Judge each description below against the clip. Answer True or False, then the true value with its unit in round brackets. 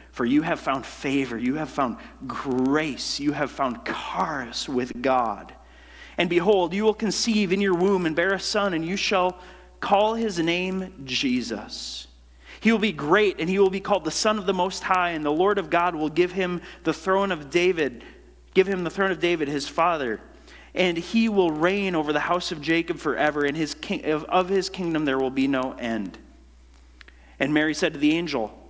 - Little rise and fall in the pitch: False (4.7 semitones)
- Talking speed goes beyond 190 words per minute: True (205 wpm)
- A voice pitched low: False (175 Hz)